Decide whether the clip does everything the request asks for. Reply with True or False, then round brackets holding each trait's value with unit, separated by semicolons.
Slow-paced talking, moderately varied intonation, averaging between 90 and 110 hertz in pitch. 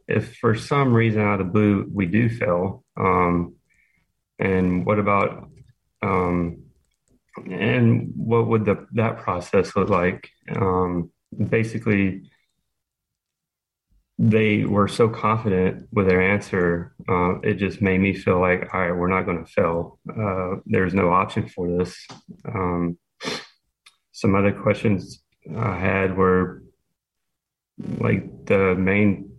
True (130 wpm; 3.3 semitones; 95 Hz)